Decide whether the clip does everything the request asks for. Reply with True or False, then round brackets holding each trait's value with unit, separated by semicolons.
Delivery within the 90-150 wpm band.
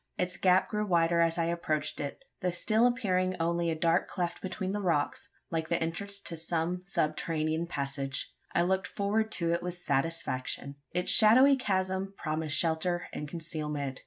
False (165 wpm)